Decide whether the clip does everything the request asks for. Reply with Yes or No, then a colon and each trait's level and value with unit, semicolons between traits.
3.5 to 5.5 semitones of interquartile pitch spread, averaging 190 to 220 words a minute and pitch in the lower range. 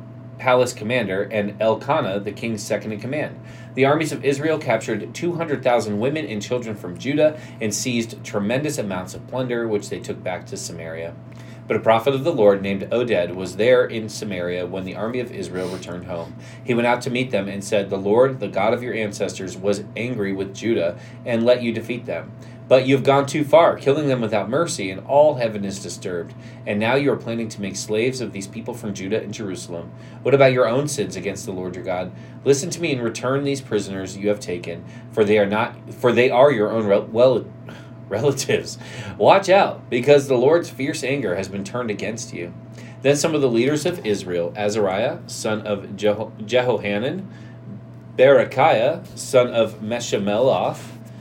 Yes: average, 4.0 semitones; average, 195 wpm; low, 115 Hz